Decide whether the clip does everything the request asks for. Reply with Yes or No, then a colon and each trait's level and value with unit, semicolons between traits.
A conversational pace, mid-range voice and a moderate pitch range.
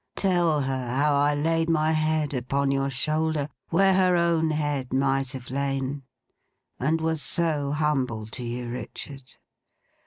Yes: average, 145 wpm; medium, 145 Hz; average, 3.0 semitones